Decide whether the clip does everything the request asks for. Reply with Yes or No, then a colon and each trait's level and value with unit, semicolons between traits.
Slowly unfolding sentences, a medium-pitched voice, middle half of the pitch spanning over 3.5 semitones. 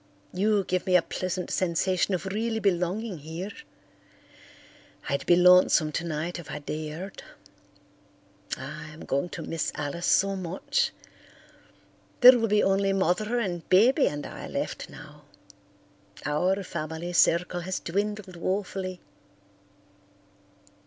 No: slow, 120 wpm; medium, 180 Hz; average, 2.9 semitones